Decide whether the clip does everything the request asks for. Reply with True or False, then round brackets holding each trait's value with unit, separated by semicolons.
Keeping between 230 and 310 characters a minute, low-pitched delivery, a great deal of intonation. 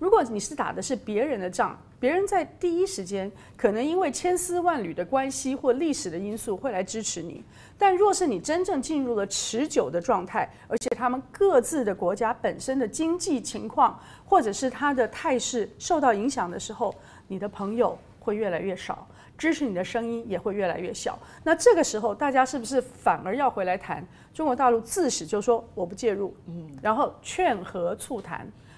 False (290 characters per minute; 245 Hz; 7.1 semitones)